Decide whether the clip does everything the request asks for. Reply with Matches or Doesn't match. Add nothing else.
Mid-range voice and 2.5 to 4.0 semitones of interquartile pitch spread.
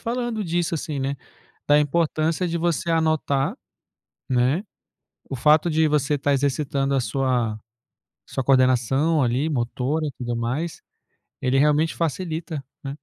Matches